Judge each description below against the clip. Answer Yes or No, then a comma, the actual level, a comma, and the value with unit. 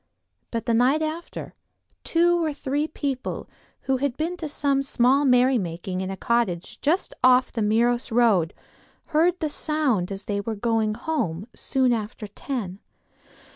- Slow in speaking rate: No, average, 150 wpm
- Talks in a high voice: Yes, high, 245 Hz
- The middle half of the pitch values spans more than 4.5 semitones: Yes, average, 5.3 semitones